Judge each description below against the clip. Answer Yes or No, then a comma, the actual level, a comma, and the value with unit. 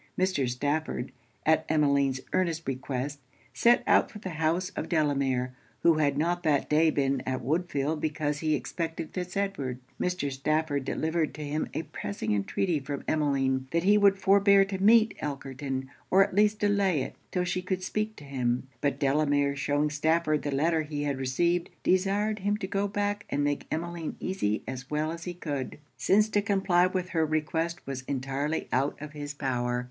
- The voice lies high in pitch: No, medium, 155 Hz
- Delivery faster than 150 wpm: Yes, average, 180 wpm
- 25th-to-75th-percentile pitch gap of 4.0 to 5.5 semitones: Yes, average, 4.7 semitones